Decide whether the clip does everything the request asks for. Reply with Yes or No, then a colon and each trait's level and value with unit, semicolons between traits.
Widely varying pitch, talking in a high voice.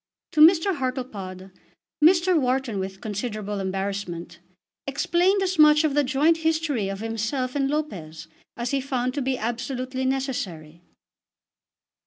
Yes: wide, 6.9 semitones; very high, 255 Hz